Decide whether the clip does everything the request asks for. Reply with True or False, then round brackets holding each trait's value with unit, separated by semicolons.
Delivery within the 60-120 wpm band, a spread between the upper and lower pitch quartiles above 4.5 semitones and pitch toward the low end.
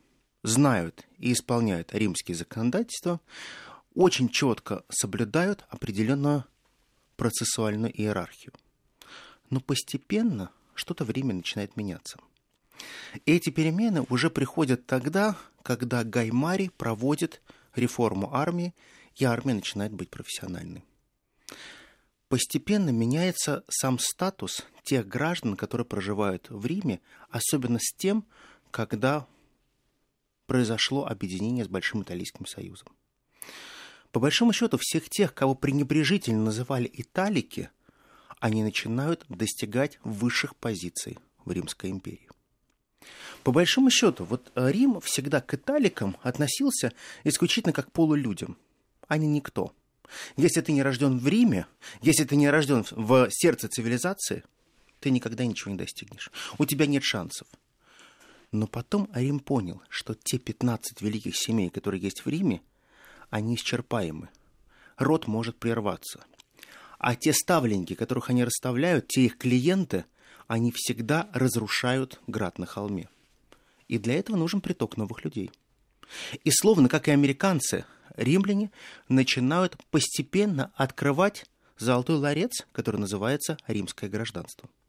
True (115 wpm; 5.5 semitones; 130 Hz)